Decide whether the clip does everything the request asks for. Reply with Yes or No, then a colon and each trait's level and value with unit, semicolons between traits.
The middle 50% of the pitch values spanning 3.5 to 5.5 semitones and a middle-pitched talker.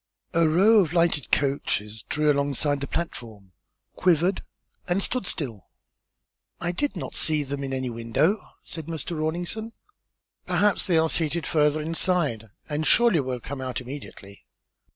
Yes: average, 4.4 semitones; medium, 155 Hz